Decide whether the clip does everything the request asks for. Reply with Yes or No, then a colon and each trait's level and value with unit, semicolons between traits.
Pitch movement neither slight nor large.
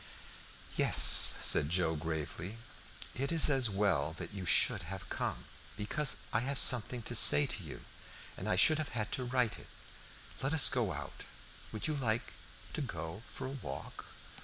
No: wide, 6.9 semitones